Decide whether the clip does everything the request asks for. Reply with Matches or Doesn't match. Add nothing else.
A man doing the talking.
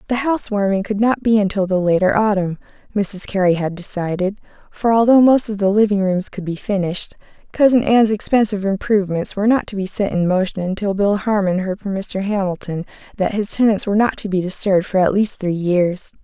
Doesn't match